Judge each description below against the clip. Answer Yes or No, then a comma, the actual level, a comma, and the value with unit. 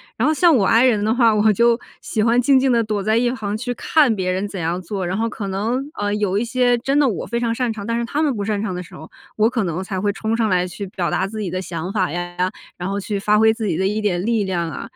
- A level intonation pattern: No, average, 3.6 semitones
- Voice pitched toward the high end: Yes, high, 210 Hz